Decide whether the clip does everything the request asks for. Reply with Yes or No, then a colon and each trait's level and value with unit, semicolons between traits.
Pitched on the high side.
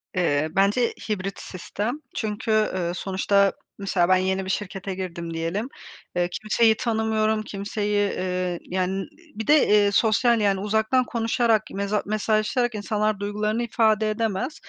Yes: high, 205 Hz